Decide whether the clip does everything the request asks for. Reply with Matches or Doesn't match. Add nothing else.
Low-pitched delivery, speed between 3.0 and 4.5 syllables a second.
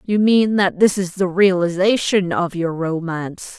Doesn't match